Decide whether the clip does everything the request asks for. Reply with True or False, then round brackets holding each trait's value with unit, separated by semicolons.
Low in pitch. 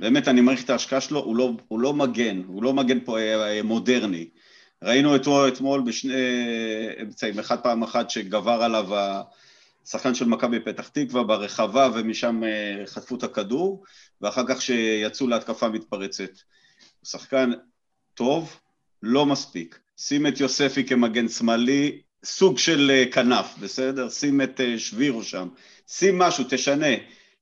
True (125 Hz)